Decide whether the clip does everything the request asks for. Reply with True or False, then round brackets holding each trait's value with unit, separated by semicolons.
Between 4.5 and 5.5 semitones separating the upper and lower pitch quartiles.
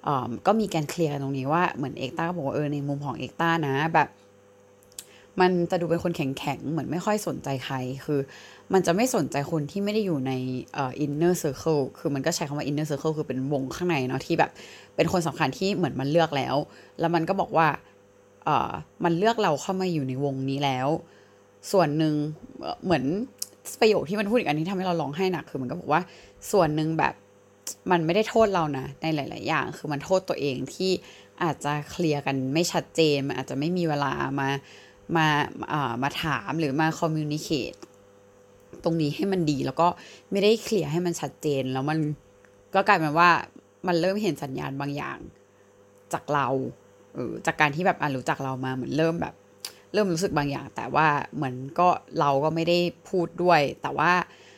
False (4.1 semitones)